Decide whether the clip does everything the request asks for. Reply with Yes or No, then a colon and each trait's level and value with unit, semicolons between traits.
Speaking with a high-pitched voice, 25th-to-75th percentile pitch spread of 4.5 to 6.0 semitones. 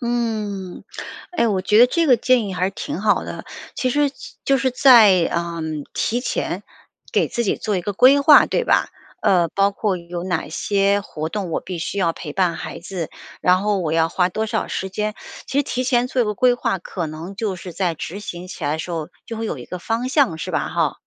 Yes: high, 200 Hz; average, 5.2 semitones